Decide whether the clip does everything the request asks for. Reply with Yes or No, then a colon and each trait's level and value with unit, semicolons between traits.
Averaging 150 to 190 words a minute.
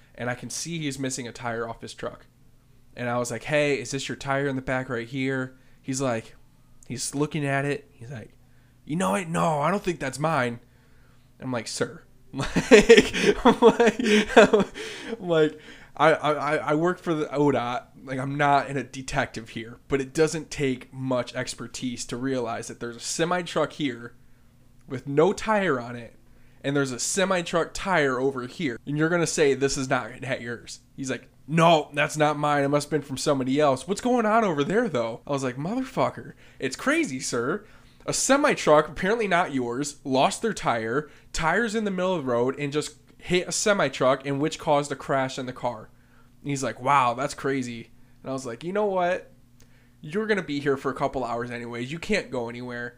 No: fast, 205 wpm